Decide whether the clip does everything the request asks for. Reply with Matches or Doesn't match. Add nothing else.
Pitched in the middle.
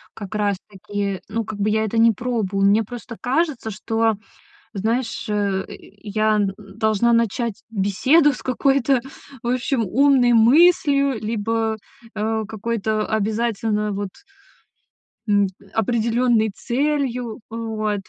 Doesn't match